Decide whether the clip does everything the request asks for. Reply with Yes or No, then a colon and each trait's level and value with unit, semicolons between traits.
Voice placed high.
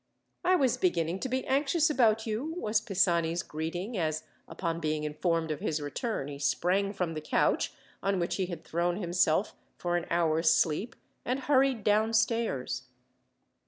No: medium, 180 Hz